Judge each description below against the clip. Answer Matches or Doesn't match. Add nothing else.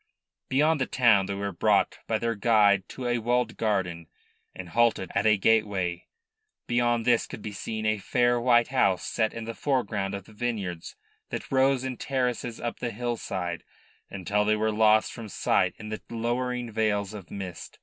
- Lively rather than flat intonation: Doesn't match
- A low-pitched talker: Matches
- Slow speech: Doesn't match